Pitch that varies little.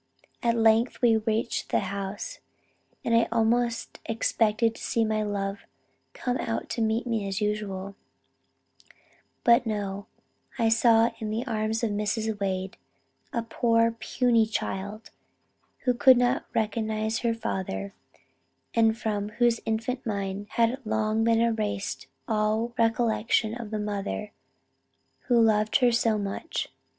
Yes: narrow, 1.8 semitones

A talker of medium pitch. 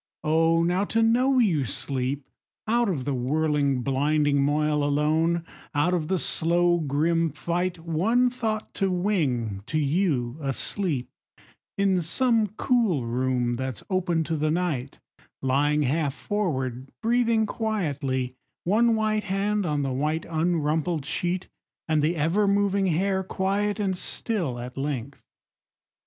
Yes: medium, 165 Hz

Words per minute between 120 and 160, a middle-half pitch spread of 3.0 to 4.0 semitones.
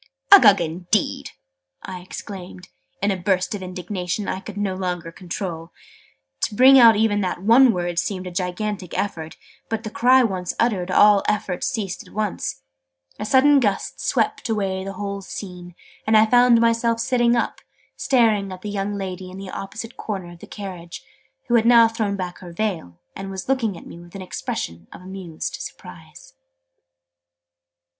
No: average, 170 wpm; average, 3.5 semitones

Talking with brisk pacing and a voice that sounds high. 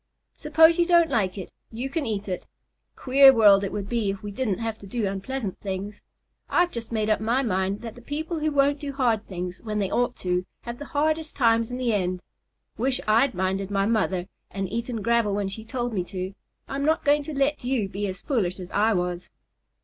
Yes: fast, 220 wpm; high, 225 Hz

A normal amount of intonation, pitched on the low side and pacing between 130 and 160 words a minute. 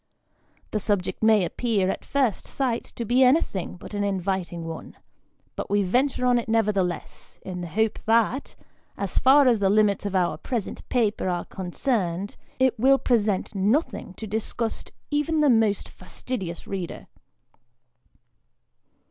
No: average, 4.5 semitones; high, 215 Hz; average, 145 wpm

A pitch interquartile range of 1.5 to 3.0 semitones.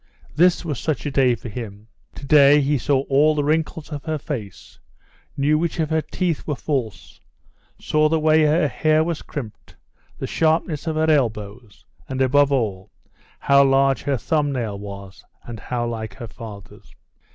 No: average, 4.7 semitones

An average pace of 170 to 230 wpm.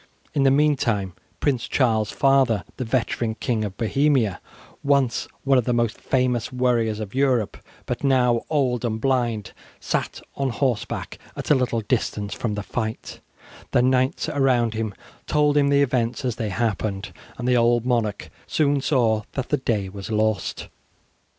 No: average, 160 wpm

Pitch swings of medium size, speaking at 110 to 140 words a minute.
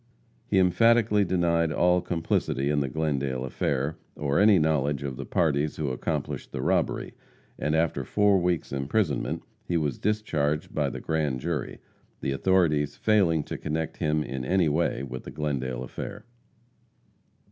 No: average, 4.0 semitones; average, 150 wpm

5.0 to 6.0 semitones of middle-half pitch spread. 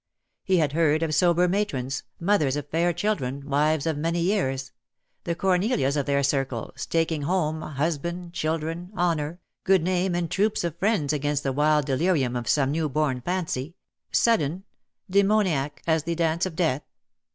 No: average, 3.6 semitones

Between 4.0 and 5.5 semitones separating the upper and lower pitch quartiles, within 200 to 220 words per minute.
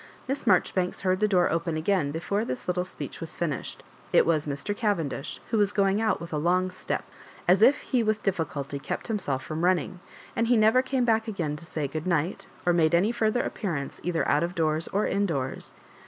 Yes: average, 5.1 semitones; fast, 205 wpm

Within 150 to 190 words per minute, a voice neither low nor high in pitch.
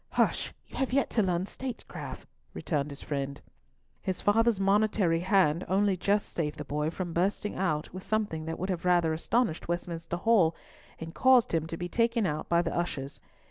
Yes: average, 180 wpm; medium, 175 Hz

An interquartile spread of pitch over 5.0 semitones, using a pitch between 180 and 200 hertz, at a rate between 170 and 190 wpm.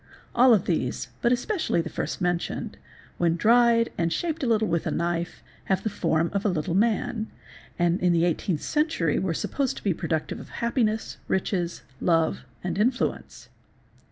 Yes: wide, 5.6 semitones; medium, 185 Hz; average, 175 wpm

